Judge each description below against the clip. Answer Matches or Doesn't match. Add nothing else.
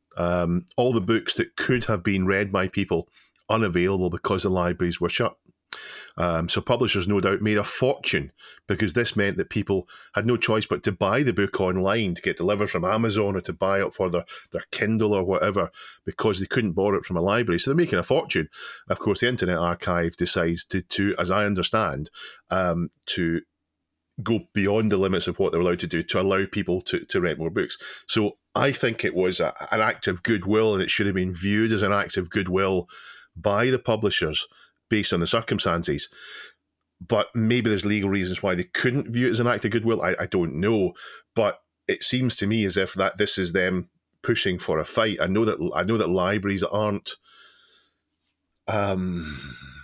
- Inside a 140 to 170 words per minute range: Doesn't match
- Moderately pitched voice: Doesn't match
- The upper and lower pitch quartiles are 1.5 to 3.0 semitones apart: Doesn't match